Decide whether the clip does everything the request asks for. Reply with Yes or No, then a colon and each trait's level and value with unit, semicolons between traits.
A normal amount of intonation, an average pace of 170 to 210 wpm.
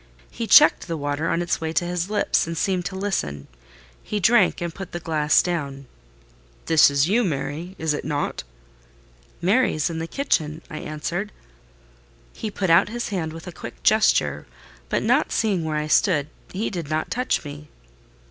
Yes: average, 3.9 semitones; average, 180 wpm